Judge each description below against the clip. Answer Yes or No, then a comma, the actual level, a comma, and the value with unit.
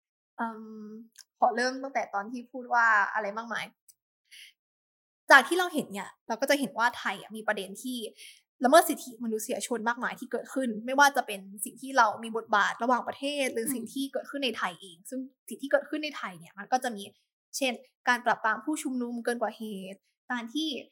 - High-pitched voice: Yes, high, 240 Hz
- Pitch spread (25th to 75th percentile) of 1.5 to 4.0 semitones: Yes, average, 3.5 semitones